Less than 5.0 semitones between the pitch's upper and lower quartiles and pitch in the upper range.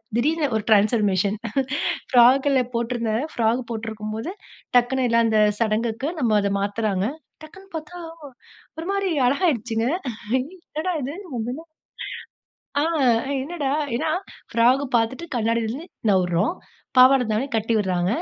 Yes: average, 4.1 semitones; high, 235 Hz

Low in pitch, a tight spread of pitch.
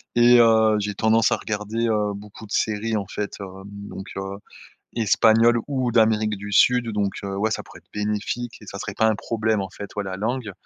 Yes: low, 105 Hz; narrow, 1.8 semitones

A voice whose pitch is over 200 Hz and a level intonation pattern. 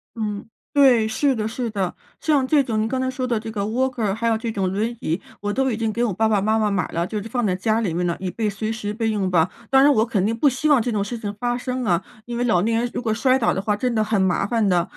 No: high, 220 Hz; average, 3.0 semitones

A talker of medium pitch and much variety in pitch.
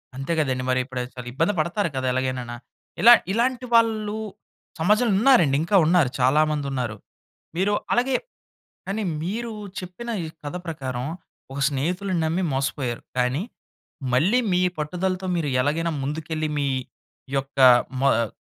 Yes: medium, 160 Hz; wide, 6.9 semitones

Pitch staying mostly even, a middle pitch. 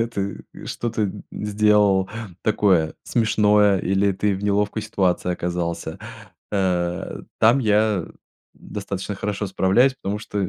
No: narrow, 1.9 semitones; low, 100 Hz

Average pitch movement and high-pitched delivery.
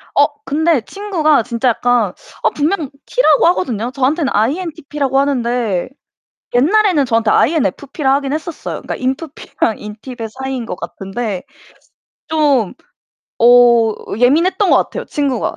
Yes: average, 4.7 semitones; very high, 265 Hz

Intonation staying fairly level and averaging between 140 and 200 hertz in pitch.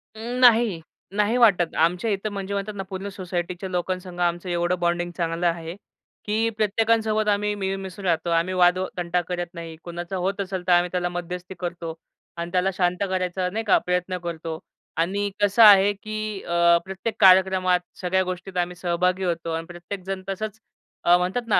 Yes: narrow, 2.3 semitones; medium, 185 Hz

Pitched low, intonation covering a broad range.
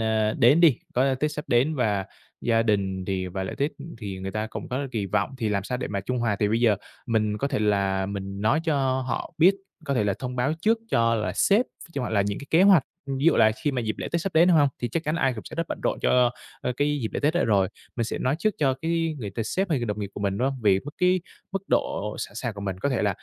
Yes: low, 120 Hz; wide, 6.0 semitones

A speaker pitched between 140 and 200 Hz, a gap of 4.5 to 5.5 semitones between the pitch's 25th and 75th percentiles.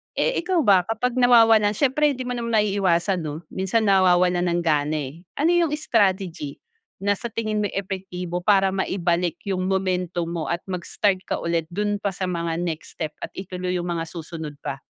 No: medium, 185 Hz; average, 3.5 semitones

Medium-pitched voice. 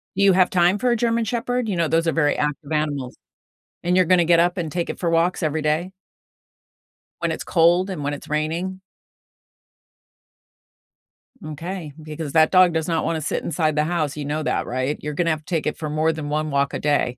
Yes: medium, 160 Hz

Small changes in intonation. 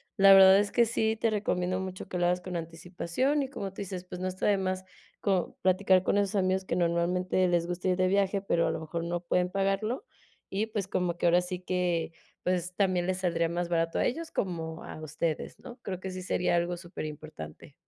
Yes: narrow, 2.1 semitones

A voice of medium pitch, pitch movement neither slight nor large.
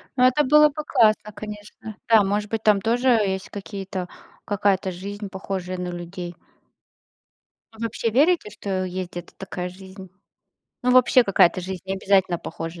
No: high, 195 Hz; average, 3.0 semitones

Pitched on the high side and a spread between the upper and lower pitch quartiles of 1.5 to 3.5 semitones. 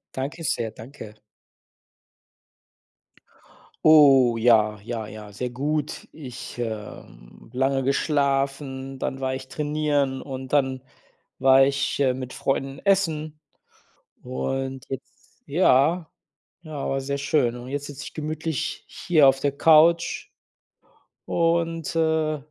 No: low, 135 Hz; average, 2.8 semitones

